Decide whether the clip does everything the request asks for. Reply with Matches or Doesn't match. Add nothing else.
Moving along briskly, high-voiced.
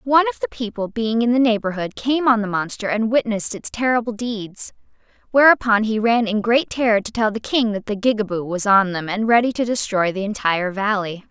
Matches